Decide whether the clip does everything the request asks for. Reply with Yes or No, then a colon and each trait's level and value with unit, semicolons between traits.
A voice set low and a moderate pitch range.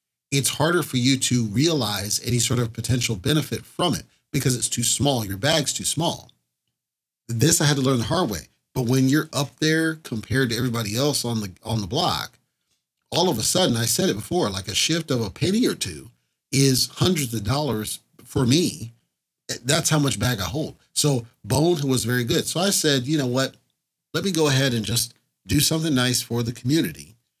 Yes: low, 130 Hz; average, 4.1 semitones